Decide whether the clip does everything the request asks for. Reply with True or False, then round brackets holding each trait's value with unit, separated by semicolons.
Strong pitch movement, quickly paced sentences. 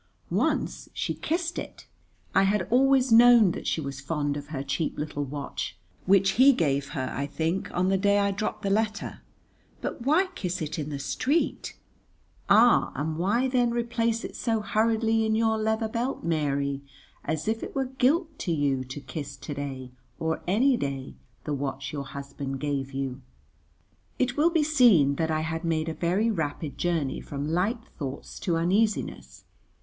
False (8.0 semitones; 175 wpm)